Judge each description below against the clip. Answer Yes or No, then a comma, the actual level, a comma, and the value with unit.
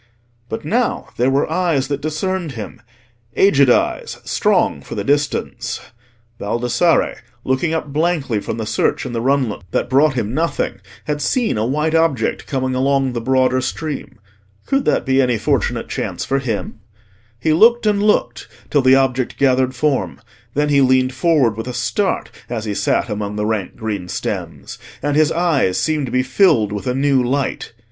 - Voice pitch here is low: Yes, low, 130 Hz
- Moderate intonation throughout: Yes, average, 4.1 semitones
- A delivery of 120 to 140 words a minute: No, average, 170 wpm